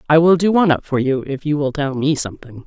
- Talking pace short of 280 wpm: No, fast, 290 wpm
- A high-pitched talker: No, medium, 145 Hz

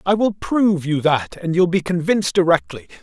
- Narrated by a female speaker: No, male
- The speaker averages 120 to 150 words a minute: No, average, 200 wpm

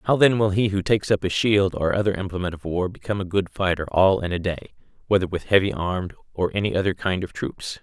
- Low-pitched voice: Yes, very low, 95 Hz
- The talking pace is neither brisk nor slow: No, fast, 245 wpm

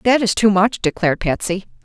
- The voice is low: No, high, 200 Hz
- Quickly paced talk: No, average, 195 wpm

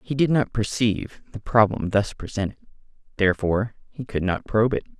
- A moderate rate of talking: Yes, average, 170 wpm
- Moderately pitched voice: No, low, 110 Hz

